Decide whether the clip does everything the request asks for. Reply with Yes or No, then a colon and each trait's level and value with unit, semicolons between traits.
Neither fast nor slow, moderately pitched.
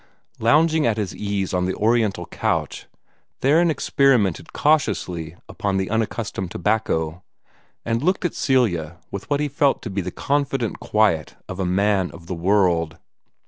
No: average, 150 wpm; low, 105 Hz